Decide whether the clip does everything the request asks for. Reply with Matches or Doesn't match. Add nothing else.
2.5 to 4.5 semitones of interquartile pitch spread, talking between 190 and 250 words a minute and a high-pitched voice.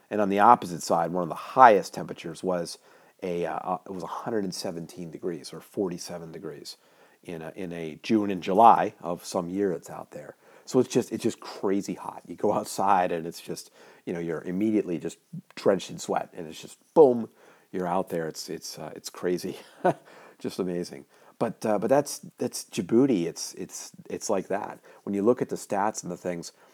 Doesn't match